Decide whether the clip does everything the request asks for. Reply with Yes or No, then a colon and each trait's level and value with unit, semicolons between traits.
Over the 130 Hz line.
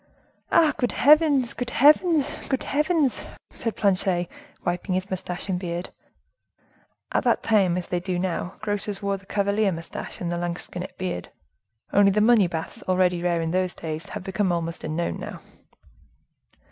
Yes: high, 190 Hz